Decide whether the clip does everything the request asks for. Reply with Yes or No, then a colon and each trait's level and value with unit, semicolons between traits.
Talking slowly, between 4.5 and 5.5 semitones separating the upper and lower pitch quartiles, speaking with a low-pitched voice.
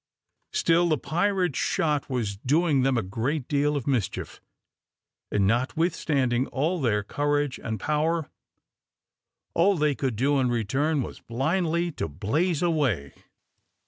No: slow, 130 wpm; average, 4.9 semitones; medium, 145 Hz